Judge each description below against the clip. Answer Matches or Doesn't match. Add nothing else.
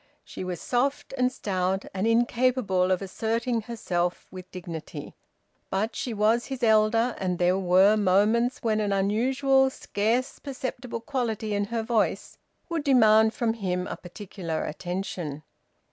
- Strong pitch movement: Doesn't match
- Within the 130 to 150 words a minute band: Matches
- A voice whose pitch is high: Matches